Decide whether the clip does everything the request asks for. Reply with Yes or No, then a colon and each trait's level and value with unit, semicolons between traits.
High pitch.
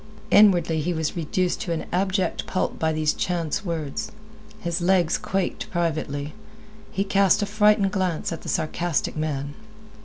No: medium, 175 Hz